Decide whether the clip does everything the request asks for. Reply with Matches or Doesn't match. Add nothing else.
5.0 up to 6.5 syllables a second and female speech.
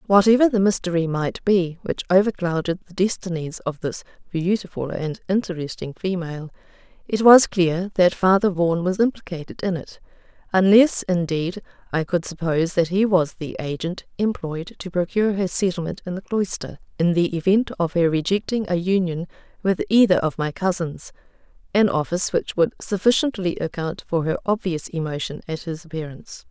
Matches